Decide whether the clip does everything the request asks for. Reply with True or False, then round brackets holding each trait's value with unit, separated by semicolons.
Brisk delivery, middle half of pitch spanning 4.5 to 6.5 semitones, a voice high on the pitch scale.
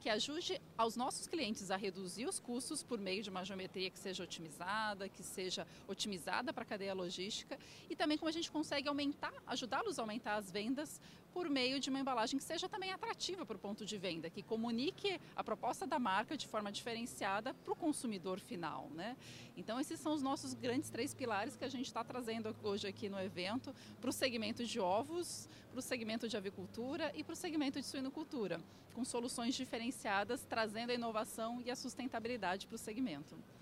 True (195 wpm; 5.1 semitones; 240 Hz)